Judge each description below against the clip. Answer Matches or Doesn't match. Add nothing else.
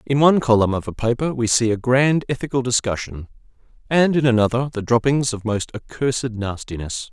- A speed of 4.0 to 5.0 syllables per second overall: Doesn't match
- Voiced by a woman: Doesn't match